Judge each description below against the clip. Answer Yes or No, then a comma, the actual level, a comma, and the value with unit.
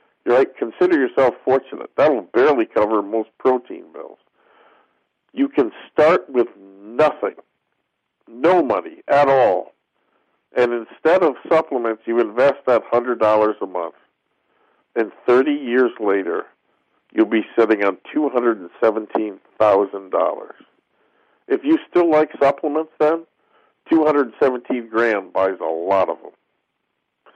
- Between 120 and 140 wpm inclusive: Yes, slow, 135 wpm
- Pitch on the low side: Yes, low, 130 Hz